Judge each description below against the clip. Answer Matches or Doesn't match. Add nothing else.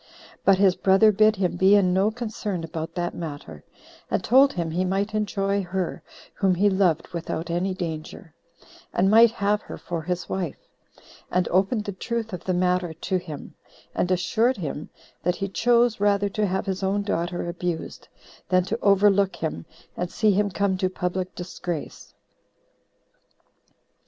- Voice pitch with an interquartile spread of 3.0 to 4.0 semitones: Doesn't match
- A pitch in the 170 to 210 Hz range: Matches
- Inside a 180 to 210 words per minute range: Doesn't match